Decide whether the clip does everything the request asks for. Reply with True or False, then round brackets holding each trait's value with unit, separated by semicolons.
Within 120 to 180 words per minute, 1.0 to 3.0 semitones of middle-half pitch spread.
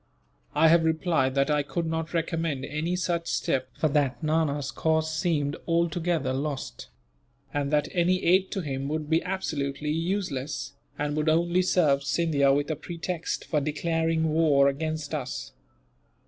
True (150 wpm; 2.7 semitones)